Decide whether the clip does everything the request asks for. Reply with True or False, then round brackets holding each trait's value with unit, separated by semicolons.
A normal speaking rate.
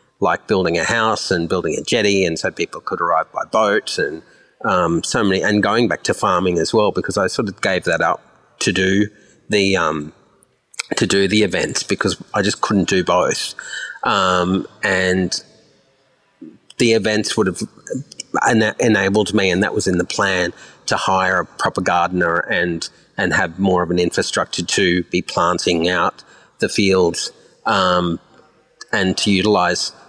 True (170 wpm)